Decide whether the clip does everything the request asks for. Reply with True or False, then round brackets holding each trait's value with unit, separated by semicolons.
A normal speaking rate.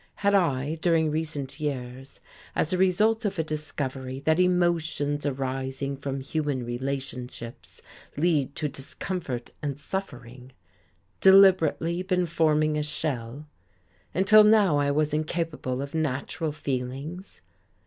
False (120 wpm)